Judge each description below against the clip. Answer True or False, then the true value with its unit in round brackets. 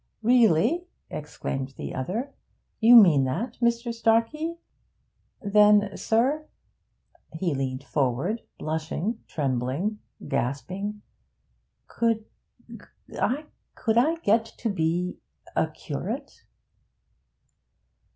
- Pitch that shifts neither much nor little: False (6.9 semitones)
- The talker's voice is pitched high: True (210 Hz)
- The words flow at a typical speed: False (80 wpm)